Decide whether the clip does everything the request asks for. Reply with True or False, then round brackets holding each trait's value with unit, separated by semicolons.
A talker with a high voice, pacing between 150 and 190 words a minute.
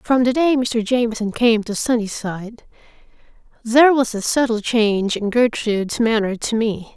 True (230 Hz; 155 wpm)